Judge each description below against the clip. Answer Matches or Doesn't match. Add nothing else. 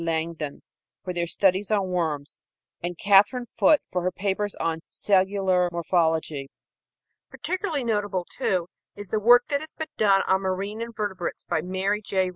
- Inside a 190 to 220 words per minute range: Doesn't match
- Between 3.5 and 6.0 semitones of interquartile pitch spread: Doesn't match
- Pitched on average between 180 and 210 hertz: Matches